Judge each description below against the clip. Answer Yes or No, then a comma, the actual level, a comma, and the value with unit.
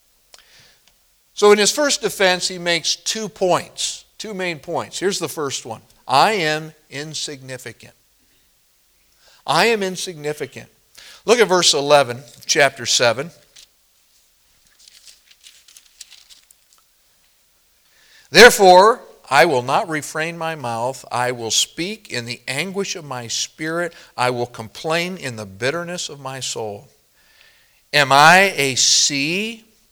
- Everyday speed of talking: No, slow, 115 wpm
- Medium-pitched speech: Yes, medium, 155 Hz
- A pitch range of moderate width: No, wide, 6.3 semitones